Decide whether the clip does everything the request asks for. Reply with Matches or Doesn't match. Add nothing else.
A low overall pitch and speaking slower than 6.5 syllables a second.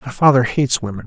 Doesn't match